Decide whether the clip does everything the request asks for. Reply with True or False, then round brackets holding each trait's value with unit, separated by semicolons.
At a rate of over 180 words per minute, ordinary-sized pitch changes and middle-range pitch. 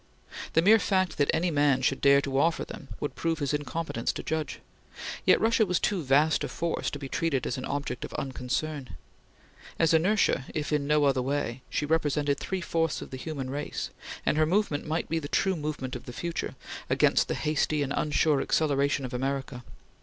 True (200 wpm; 3.0 semitones; 150 Hz)